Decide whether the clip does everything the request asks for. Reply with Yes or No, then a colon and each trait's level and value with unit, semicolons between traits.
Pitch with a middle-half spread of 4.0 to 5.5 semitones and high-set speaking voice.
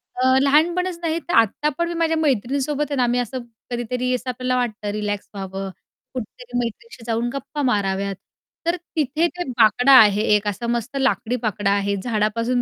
Yes: average, 4.9 semitones; high, 245 Hz